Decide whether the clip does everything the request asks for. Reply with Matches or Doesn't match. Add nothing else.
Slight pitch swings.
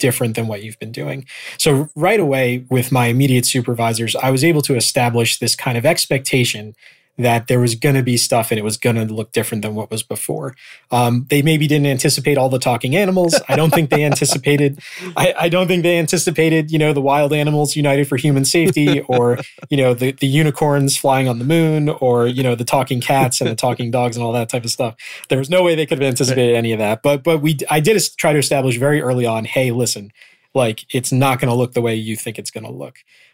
Doesn't match